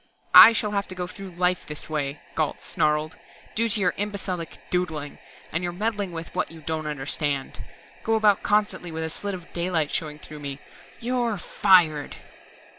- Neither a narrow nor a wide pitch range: Yes, average, 4.7 semitones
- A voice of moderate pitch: Yes, medium, 175 Hz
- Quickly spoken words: No, average, 170 wpm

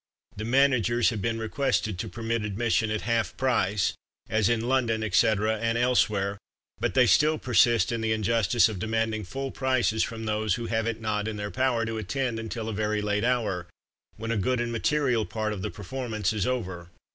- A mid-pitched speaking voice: No, low, 110 Hz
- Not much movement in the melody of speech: Yes, narrow, 2.0 semitones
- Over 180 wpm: Yes, average, 190 wpm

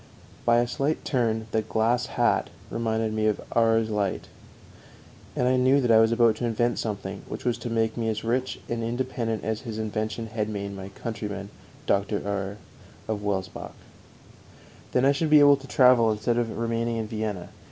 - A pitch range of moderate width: No, narrow, 2.0 semitones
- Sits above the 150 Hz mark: No, low, 115 Hz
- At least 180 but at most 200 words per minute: Yes, average, 185 wpm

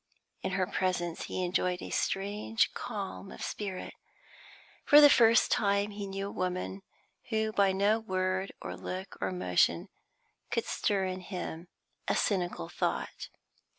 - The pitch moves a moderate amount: No, narrow, 1.9 semitones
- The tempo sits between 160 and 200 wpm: No, average, 145 wpm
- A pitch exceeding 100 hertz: Yes, high, 190 Hz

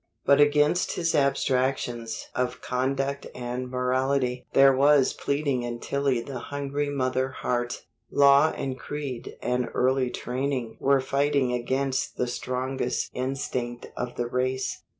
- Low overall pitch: Yes, low, 130 Hz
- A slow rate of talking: Yes, slow, 130 wpm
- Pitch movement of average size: No, narrow, 1.9 semitones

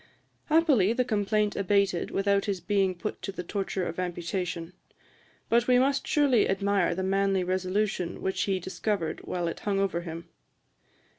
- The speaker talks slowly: No, average, 155 wpm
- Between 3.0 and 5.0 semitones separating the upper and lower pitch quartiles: No, narrow, 2.5 semitones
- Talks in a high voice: Yes, high, 195 Hz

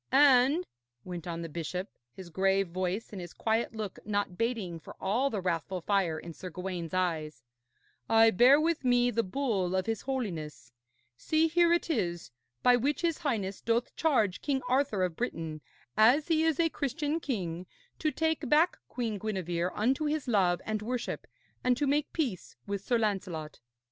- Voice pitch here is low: No, high, 215 Hz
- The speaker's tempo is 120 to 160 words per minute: No, average, 175 wpm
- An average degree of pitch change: No, wide, 7.0 semitones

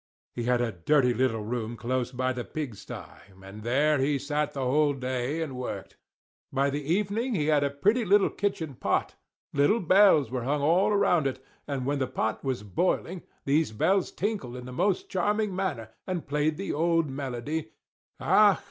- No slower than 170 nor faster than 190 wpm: Yes, average, 185 wpm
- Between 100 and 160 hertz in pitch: Yes, medium, 140 Hz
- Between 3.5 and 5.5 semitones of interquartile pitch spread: Yes, average, 5.1 semitones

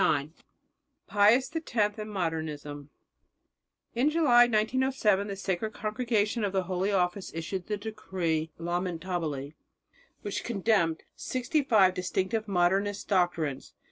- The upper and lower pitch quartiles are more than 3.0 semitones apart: Yes, average, 3.9 semitones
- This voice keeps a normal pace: No, slow, 110 wpm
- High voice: Yes, high, 195 Hz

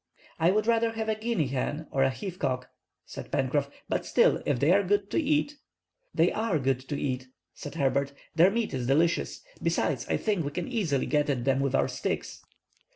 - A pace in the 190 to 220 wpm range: Yes, fast, 205 wpm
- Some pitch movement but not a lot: No, wide, 7.9 semitones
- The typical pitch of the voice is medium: Yes, medium, 155 Hz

